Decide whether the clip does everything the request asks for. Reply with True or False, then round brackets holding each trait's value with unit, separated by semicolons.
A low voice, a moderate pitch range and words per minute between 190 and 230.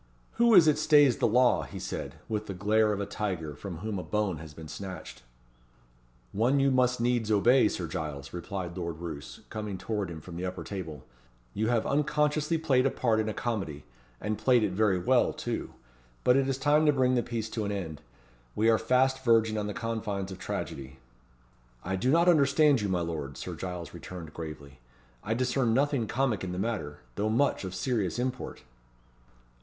False (110 Hz; 6.0 semitones; 195 wpm)